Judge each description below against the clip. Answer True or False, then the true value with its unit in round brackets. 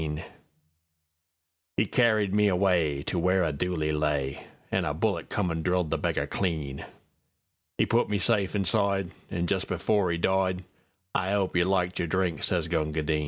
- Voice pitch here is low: True (90 Hz)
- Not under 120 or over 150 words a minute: True (145 wpm)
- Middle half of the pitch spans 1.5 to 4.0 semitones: True (3.1 semitones)